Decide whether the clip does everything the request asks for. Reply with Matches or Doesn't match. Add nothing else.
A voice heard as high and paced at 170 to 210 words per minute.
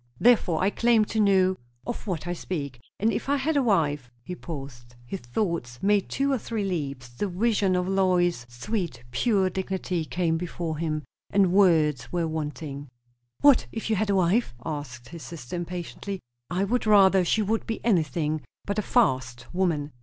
Doesn't match